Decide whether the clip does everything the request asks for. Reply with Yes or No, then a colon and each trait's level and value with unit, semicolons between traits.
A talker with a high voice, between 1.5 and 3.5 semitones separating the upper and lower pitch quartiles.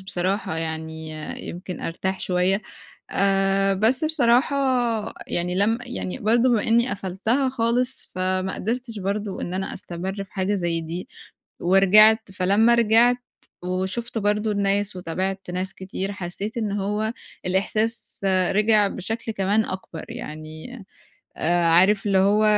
Yes: high, 195 Hz; average, 3.1 semitones